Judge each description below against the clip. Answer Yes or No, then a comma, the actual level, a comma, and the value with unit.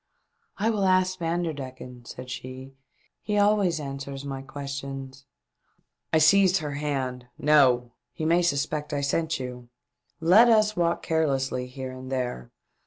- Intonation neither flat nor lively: Yes, average, 4.4 semitones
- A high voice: No, medium, 140 Hz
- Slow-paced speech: No, average, 155 wpm